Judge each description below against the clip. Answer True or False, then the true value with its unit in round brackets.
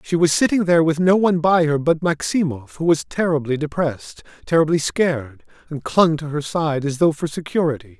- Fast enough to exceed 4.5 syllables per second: True (5.5 syllables/s)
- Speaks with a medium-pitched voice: True (155 Hz)